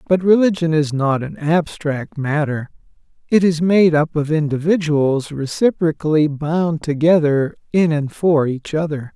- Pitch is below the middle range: No, medium, 155 Hz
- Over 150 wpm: No, average, 140 wpm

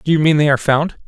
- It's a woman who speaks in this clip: No, male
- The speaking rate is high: Yes, fast, 335 wpm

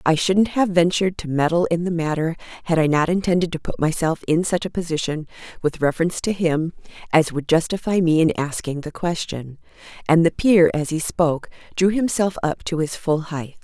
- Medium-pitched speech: Yes, medium, 165 Hz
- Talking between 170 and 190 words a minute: No, average, 200 wpm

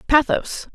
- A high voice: Yes, very high, 300 Hz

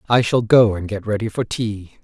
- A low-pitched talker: Yes, low, 110 Hz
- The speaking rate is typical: No, fast, 235 wpm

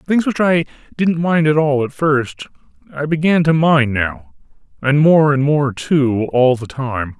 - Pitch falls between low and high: Yes, medium, 145 Hz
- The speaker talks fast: No, average, 175 wpm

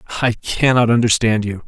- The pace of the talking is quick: No, average, 145 wpm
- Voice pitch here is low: Yes, low, 115 Hz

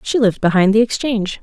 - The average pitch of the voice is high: Yes, high, 215 Hz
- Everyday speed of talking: No, fast, 210 wpm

